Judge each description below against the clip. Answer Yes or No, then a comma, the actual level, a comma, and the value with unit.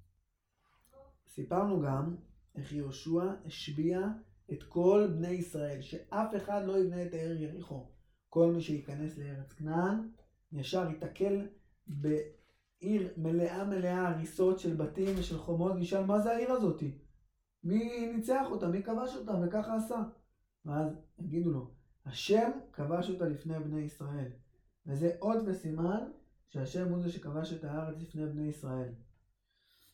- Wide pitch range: No, average, 4.3 semitones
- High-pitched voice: No, medium, 170 Hz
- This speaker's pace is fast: No, average, 130 wpm